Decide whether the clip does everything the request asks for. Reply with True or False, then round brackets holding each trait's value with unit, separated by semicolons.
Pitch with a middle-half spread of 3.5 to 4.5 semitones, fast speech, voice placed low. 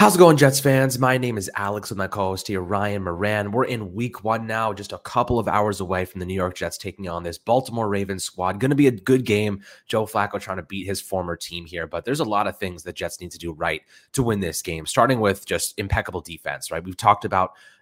True (3.8 semitones; 265 wpm; 100 Hz)